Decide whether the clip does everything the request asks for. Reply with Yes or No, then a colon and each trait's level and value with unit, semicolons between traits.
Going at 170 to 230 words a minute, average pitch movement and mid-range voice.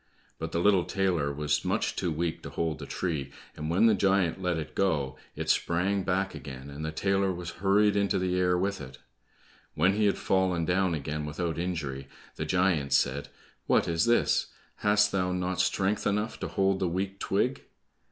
No: average, 190 wpm; average, 3.6 semitones; very low, 90 Hz